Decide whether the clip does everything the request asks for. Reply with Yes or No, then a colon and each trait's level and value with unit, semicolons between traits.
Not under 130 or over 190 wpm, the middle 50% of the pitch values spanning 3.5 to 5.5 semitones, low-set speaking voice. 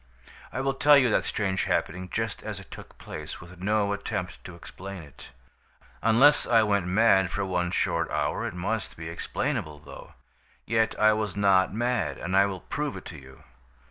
Yes: average, 185 wpm; average, 3.9 semitones; low, 100 Hz